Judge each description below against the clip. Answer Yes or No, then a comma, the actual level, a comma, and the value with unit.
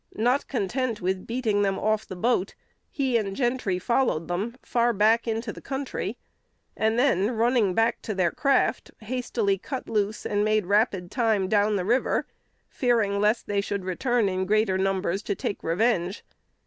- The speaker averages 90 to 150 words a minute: No, average, 165 wpm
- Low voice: No, high, 215 Hz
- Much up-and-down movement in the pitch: No, average, 3.6 semitones